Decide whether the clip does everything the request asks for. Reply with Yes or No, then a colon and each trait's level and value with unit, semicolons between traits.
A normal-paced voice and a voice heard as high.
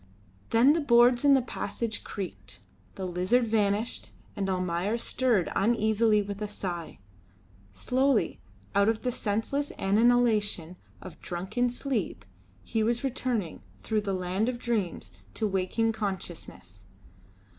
No: slow, 125 wpm; high, 215 Hz